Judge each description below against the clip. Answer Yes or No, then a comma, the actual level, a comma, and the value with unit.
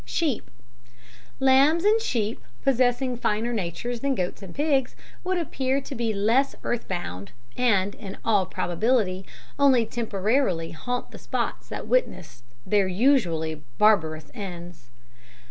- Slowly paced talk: Yes, slow, 130 wpm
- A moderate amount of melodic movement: No, wide, 6.3 semitones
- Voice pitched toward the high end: Yes, high, 225 Hz